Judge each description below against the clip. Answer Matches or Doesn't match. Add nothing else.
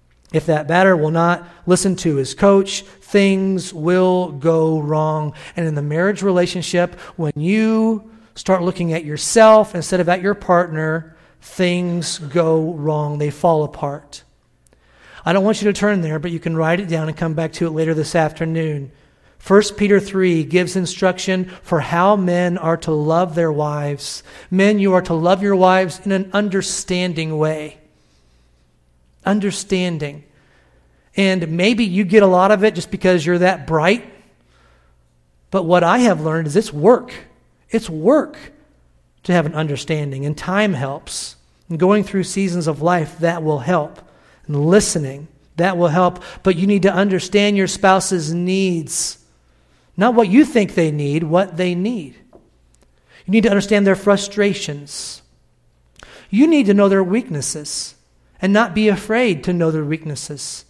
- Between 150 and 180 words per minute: Matches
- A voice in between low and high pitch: Matches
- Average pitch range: Matches